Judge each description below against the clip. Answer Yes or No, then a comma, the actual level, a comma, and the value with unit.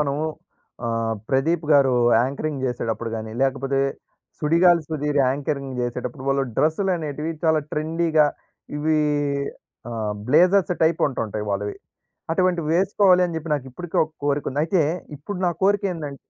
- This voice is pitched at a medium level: Yes, medium, 150 Hz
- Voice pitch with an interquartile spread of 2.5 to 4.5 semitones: Yes, average, 3.8 semitones